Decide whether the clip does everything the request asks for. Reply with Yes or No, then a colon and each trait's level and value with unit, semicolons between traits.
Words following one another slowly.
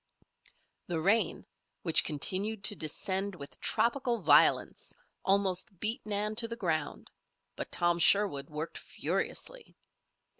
Yes: slow, 115 wpm